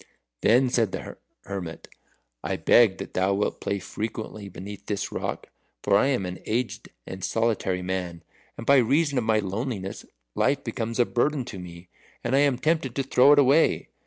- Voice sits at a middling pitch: No, low, 110 Hz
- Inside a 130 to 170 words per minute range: No, average, 180 wpm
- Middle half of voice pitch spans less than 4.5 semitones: No, average, 5.0 semitones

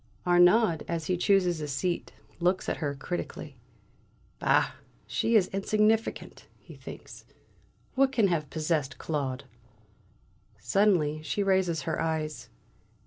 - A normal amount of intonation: Yes, average, 4.2 semitones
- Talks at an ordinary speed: No, slow, 120 wpm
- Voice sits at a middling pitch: Yes, medium, 170 Hz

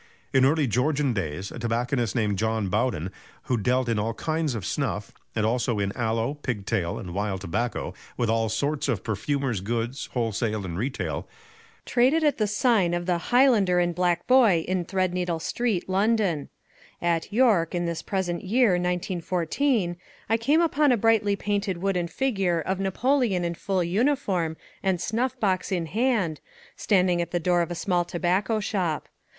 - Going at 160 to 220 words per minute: Yes, average, 165 wpm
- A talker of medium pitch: Yes, medium, 175 Hz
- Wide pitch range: Yes, wide, 8.5 semitones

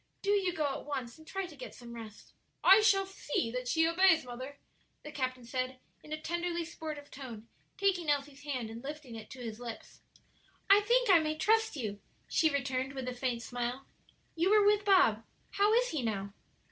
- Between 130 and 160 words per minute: No, average, 195 wpm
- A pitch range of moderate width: No, wide, 6.4 semitones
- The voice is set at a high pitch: Yes, very high, 290 Hz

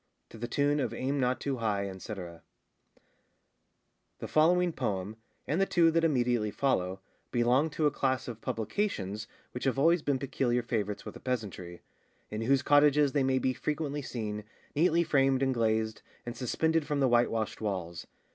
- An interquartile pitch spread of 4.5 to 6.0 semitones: Yes, average, 4.8 semitones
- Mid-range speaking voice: No, low, 130 Hz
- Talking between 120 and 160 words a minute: No, average, 170 wpm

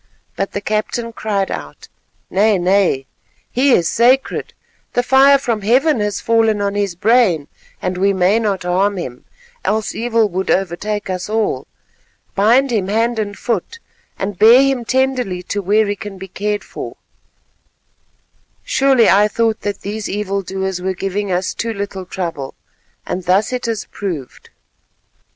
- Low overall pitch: No, high, 205 Hz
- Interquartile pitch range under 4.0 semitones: Yes, average, 3.3 semitones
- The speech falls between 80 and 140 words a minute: No, average, 155 wpm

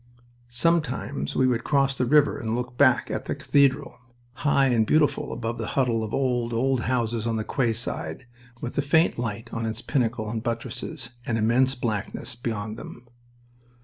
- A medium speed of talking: Yes, average, 170 wpm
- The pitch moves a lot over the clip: No, average, 2.8 semitones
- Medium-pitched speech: No, low, 120 Hz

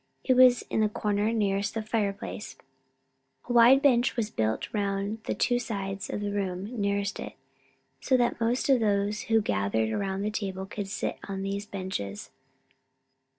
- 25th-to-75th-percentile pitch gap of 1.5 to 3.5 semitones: Yes, narrow, 2.5 semitones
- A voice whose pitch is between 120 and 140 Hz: No, high, 205 Hz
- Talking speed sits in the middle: Yes, average, 165 wpm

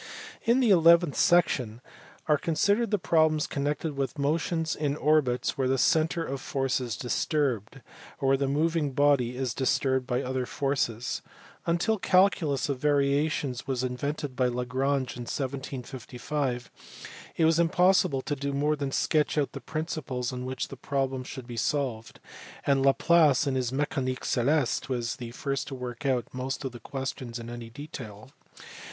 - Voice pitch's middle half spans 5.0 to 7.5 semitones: No, average, 3.2 semitones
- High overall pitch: No, low, 135 Hz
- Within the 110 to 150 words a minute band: No, average, 160 wpm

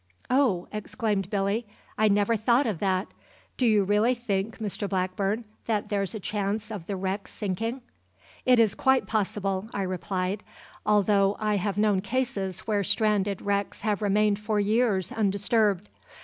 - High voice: Yes, high, 205 Hz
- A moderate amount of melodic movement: No, narrow, 2.0 semitones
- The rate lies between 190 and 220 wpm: No, average, 150 wpm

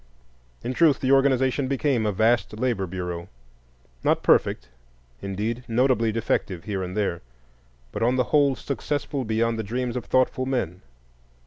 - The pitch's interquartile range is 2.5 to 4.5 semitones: No, average, 5.3 semitones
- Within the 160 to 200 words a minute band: No, average, 140 wpm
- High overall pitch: No, low, 115 Hz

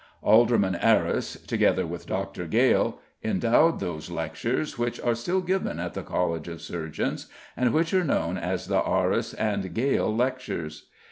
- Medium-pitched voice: No, low, 105 Hz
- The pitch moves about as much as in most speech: No, wide, 5.8 semitones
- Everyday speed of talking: Yes, average, 150 wpm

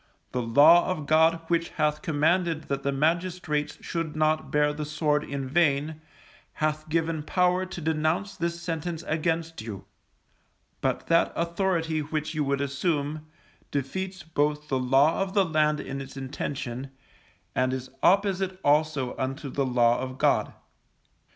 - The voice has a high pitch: No, medium, 155 Hz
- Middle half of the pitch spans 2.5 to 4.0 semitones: Yes, average, 3.1 semitones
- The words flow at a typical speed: Yes, average, 145 wpm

